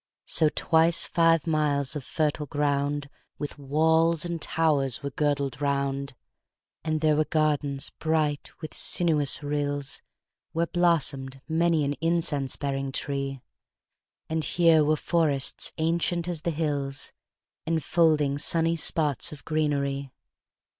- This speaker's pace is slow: Yes, slow, 125 wpm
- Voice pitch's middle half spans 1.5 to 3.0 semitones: Yes, narrow, 2.4 semitones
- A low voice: No, medium, 150 Hz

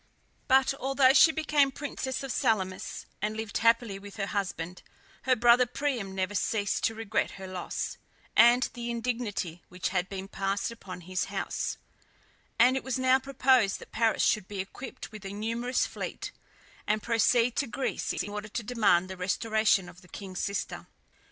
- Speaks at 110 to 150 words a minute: No, average, 170 wpm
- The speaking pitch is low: No, high, 220 Hz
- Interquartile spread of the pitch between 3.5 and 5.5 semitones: Yes, average, 4.2 semitones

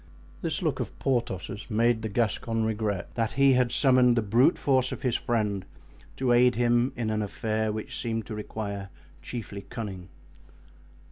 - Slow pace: No, average, 160 wpm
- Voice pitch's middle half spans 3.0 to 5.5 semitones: No, narrow, 2.4 semitones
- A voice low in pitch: Yes, low, 115 Hz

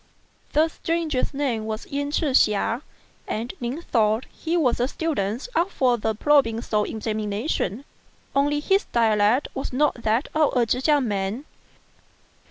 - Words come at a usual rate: Yes, average, 145 wpm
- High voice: Yes, very high, 250 Hz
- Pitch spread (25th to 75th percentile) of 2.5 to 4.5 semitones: No, average, 5.1 semitones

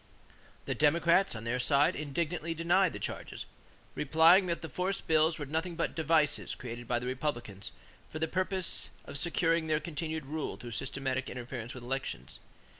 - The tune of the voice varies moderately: Yes, average, 4.2 semitones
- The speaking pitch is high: No, medium, 155 Hz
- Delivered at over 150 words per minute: Yes, average, 165 wpm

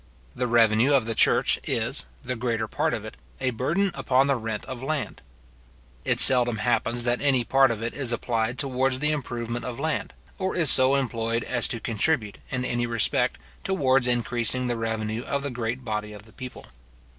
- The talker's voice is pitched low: Yes, low, 120 Hz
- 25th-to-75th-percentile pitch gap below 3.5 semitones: Yes, narrow, 2.6 semitones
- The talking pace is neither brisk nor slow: Yes, average, 190 wpm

